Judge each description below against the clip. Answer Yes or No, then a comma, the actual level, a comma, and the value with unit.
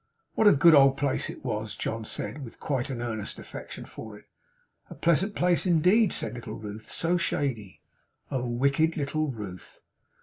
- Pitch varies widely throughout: Yes, wide, 6.2 semitones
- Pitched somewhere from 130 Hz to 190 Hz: Yes, low, 135 Hz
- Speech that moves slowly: No, average, 170 wpm